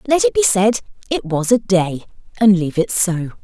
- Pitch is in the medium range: No, high, 210 Hz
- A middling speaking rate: No, fast, 210 wpm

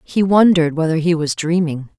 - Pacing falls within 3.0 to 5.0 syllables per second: No, 5.5 syllables/s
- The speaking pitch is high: No, medium, 165 Hz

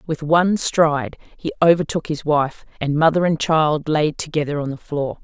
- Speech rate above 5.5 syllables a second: No, 5.0 syllables/s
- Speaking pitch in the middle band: Yes, medium, 155 Hz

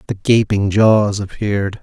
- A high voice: No, low, 100 Hz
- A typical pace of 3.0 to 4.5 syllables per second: Yes, 4.2 syllables/s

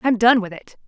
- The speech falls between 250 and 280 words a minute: Yes, fast, 275 wpm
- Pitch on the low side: No, high, 220 Hz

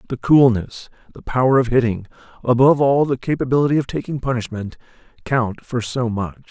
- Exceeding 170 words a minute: No, average, 155 wpm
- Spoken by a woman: No, male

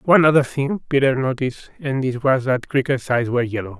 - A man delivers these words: Yes, male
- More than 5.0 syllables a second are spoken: Yes, 5.8 syllables/s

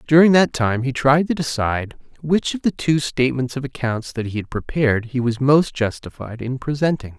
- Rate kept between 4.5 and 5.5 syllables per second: Yes, 5.3 syllables/s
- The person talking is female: No, male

